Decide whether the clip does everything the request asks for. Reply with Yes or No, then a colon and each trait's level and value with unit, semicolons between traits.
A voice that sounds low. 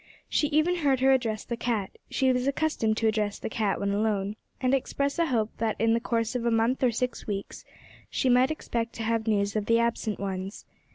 No: high, 230 Hz